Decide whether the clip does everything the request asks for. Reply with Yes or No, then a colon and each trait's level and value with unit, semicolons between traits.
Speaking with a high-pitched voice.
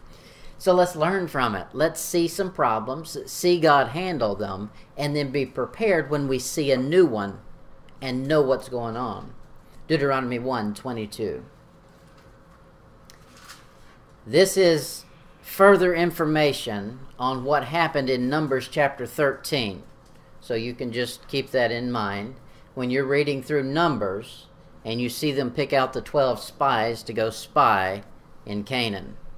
No: low, 135 Hz